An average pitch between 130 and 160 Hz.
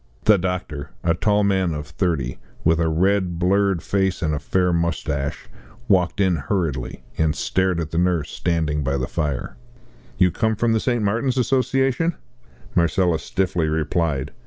No: very low, 90 Hz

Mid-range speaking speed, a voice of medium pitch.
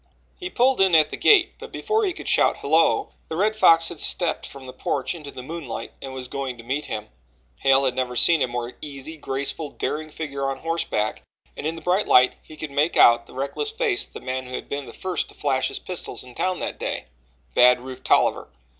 No: fast, 230 wpm; medium, 145 Hz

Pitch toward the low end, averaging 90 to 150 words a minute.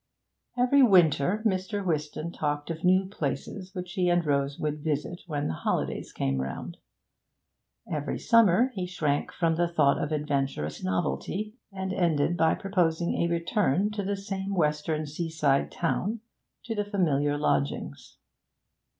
No: medium, 170 Hz; average, 140 wpm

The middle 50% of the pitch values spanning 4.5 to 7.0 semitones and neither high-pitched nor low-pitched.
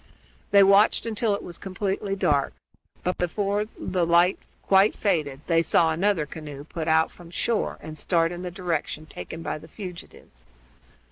No: average, 3.5 semitones; medium, 175 Hz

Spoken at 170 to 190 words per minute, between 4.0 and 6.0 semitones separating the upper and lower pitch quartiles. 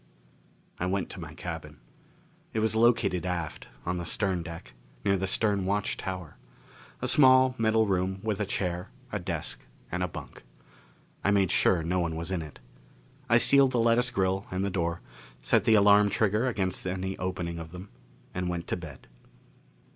No: average, 175 wpm; average, 2.8 semitones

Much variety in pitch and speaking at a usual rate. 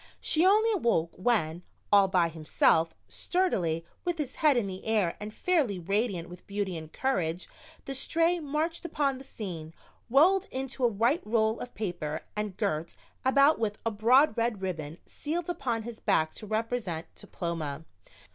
Yes: wide, 7.7 semitones; average, 160 wpm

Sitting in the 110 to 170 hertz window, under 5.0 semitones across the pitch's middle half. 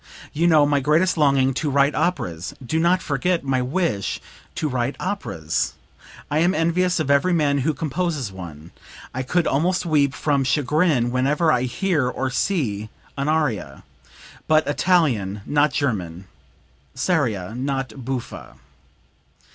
Yes: medium, 140 Hz; average, 4.4 semitones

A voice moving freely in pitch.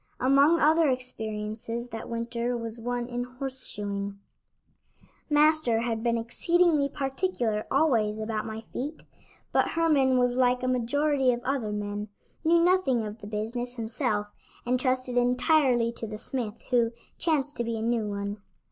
No: average, 3.3 semitones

